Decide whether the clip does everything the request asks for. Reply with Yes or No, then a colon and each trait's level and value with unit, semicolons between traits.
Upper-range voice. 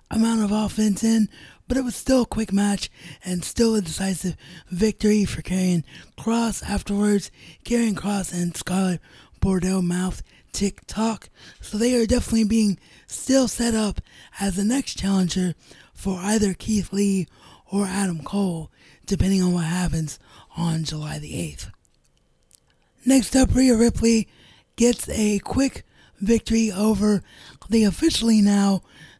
Yes: high, 200 Hz